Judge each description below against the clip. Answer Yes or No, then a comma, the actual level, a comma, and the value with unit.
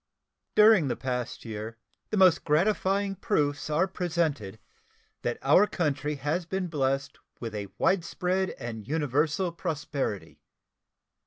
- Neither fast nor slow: No, slow, 115 wpm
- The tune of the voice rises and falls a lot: Yes, wide, 5.7 semitones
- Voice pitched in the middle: Yes, medium, 150 Hz